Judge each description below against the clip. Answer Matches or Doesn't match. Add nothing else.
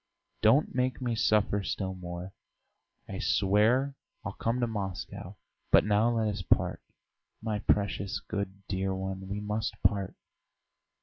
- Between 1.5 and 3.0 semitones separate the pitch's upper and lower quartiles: Matches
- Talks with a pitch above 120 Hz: Doesn't match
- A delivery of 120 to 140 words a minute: Matches